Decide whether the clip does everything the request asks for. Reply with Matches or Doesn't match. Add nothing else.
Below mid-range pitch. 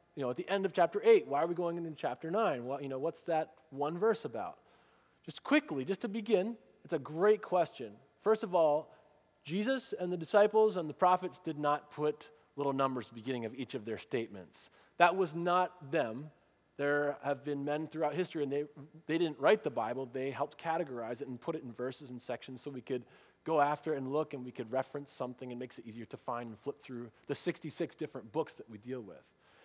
Doesn't match